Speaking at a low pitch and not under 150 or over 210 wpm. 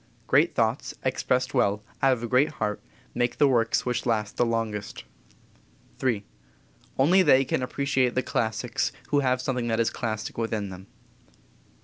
Yes: low, 120 Hz; average, 155 wpm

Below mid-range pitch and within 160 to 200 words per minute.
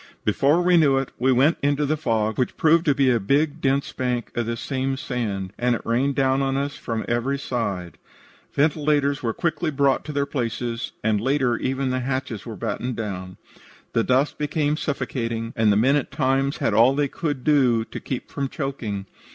Yes: low, 130 Hz; average, 195 wpm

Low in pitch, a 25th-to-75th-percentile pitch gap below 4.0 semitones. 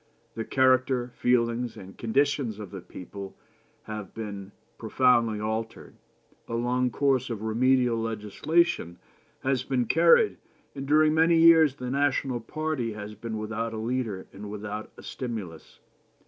Yes: low, 115 Hz; average, 3.6 semitones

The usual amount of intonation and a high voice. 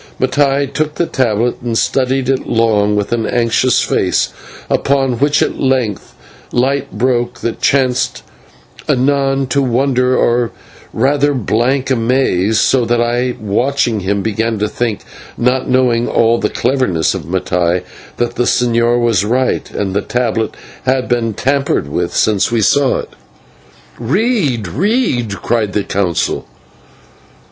No: average, 3.2 semitones; low, 120 Hz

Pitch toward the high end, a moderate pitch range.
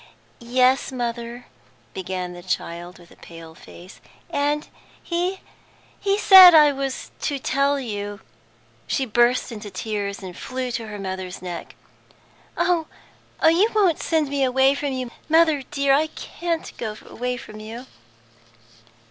No: very high, 250 Hz; wide, 6.2 semitones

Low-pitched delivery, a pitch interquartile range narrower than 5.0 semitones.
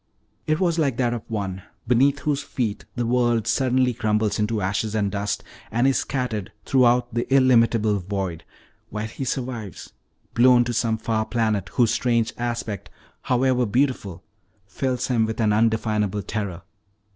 Yes: low, 115 Hz; average, 3.0 semitones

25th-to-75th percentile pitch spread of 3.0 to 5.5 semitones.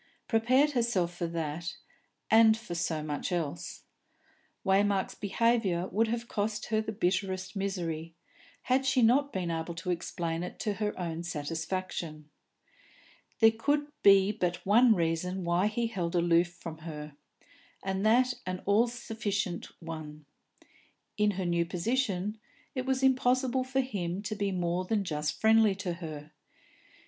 Yes: average, 4.6 semitones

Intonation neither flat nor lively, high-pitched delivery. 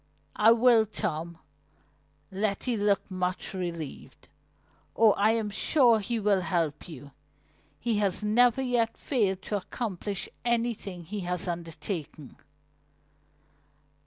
Yes: average, 4.2 semitones; high, 200 Hz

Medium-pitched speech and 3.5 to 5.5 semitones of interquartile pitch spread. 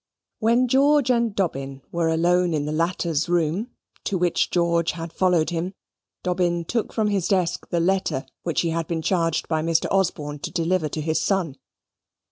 No: medium, 170 Hz; average, 2.8 semitones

